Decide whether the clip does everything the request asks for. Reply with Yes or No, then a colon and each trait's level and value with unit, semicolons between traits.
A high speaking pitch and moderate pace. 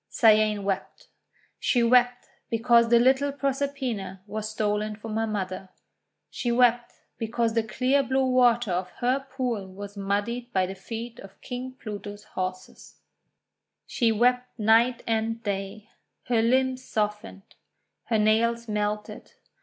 No: high, 225 Hz; slow, 130 wpm